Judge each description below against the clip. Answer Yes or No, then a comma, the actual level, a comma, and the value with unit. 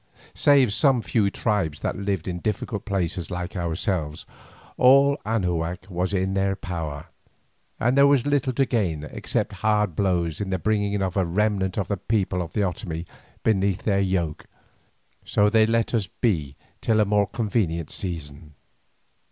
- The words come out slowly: No, average, 160 wpm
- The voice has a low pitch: Yes, very low, 95 Hz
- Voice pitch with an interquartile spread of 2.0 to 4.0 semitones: Yes, average, 3.7 semitones